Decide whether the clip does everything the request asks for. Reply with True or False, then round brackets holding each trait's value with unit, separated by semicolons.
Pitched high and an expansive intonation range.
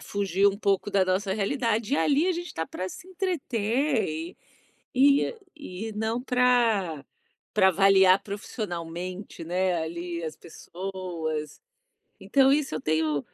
True (195 Hz; 5.8 semitones)